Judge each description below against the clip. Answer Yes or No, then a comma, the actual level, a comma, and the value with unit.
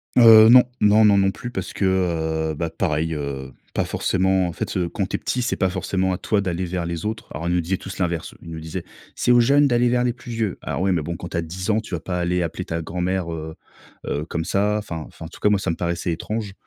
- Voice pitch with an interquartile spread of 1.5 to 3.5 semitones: No, average, 3.9 semitones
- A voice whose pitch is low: Yes, very low, 90 Hz